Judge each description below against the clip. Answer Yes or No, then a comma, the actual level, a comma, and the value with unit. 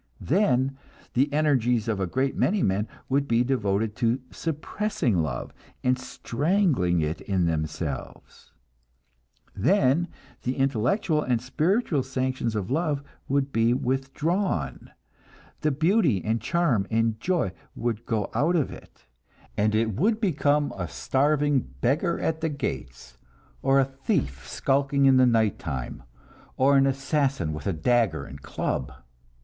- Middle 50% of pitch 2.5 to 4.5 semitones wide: No, wide, 5.5 semitones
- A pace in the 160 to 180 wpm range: No, slow, 135 wpm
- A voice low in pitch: Yes, low, 130 Hz